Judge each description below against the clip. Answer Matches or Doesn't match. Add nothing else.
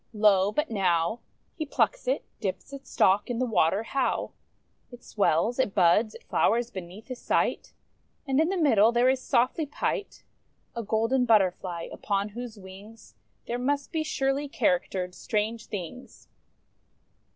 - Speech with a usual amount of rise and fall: Matches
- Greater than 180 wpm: Doesn't match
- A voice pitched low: Doesn't match